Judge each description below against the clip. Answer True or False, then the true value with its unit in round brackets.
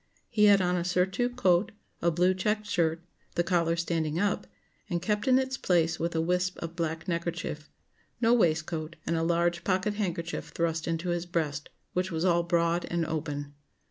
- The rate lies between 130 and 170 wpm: False (180 wpm)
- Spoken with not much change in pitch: True (2.0 semitones)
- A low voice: False (170 Hz)